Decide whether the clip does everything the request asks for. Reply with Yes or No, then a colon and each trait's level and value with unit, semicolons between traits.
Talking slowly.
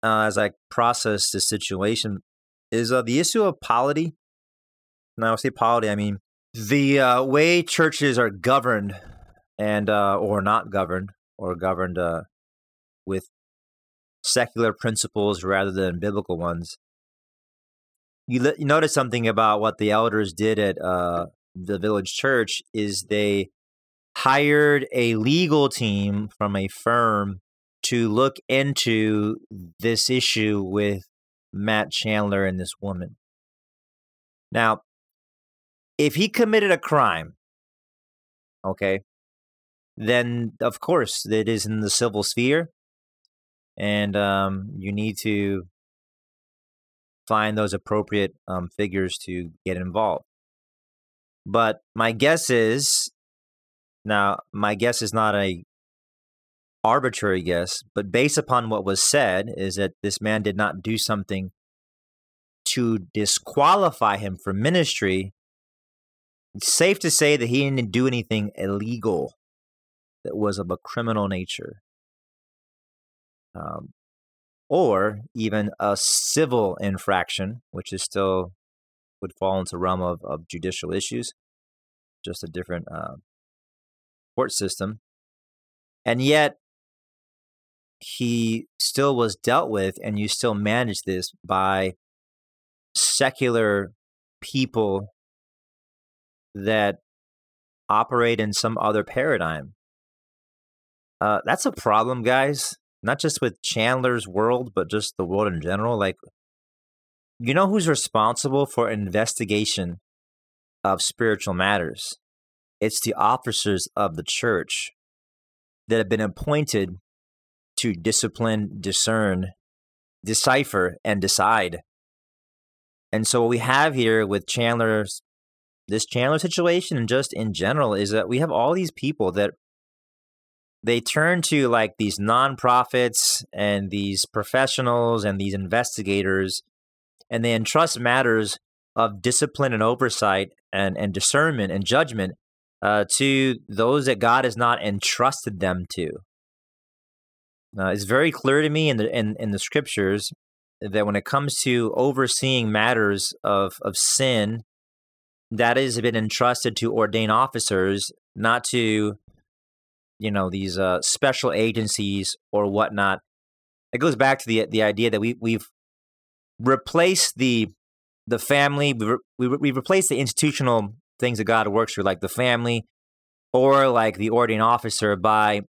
Yes: slow, 125 wpm